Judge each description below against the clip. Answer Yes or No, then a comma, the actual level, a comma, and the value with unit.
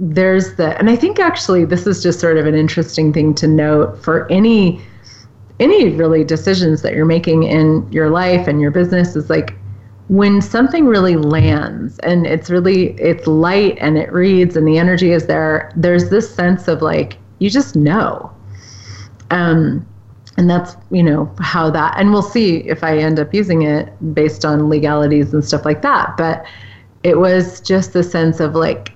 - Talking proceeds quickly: No, average, 180 wpm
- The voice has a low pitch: No, medium, 160 Hz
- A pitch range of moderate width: Yes, average, 3.0 semitones